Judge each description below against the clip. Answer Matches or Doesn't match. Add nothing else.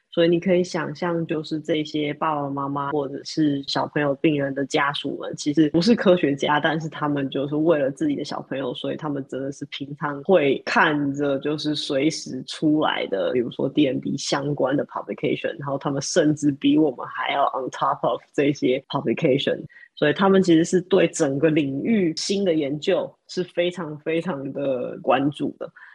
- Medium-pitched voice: Matches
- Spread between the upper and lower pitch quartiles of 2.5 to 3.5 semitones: Matches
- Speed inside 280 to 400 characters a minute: Matches